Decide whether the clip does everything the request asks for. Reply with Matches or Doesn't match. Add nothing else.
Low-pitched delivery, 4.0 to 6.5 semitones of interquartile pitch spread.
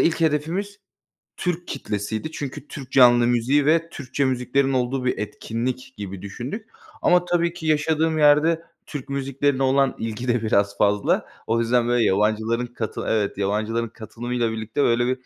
Matches